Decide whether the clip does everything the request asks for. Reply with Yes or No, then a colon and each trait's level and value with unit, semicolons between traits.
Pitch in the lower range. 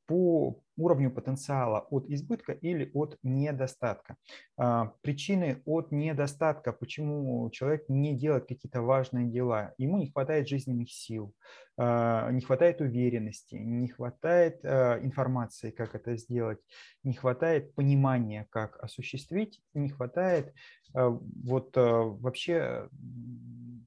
Yes: low, 130 Hz